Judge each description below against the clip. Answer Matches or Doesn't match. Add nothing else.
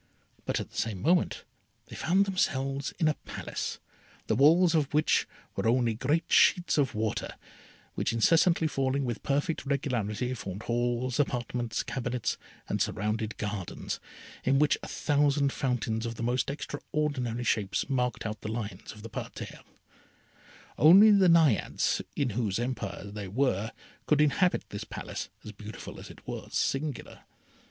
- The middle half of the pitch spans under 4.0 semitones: Doesn't match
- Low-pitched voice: Matches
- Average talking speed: Matches